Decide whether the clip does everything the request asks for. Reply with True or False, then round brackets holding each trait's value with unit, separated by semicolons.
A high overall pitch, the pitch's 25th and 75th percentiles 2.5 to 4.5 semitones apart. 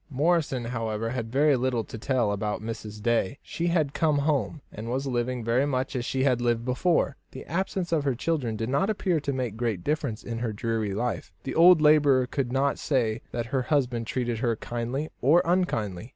False (125 Hz; 4.0 semitones)